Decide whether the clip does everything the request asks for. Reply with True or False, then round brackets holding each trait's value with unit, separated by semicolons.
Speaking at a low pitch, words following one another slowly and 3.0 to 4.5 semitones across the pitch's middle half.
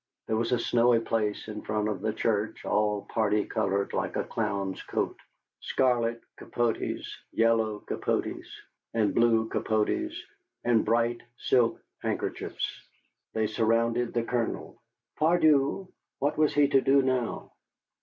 False (115 Hz; 130 wpm; 2.4 semitones)